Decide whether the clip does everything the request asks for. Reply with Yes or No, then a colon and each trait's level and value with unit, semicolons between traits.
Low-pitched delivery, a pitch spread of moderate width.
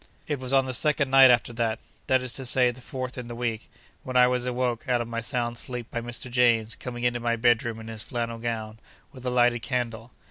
No: low, 120 Hz; narrow, 1.4 semitones